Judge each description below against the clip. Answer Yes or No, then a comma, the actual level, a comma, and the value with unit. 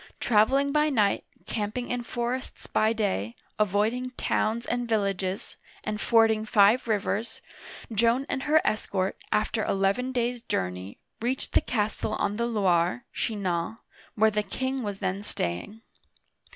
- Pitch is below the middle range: No, high, 220 Hz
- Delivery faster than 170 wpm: No, average, 140 wpm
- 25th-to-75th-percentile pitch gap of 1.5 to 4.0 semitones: Yes, average, 3.3 semitones